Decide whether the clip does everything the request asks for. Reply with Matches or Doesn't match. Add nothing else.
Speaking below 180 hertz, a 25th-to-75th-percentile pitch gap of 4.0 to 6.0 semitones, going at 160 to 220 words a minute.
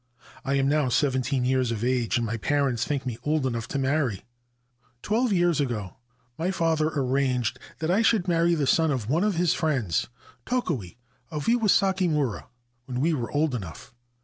Matches